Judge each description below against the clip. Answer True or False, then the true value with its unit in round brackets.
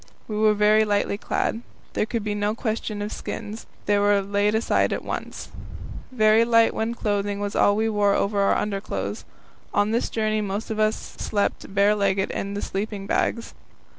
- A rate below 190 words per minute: True (175 wpm)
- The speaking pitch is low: False (210 Hz)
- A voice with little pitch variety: True (1.2 semitones)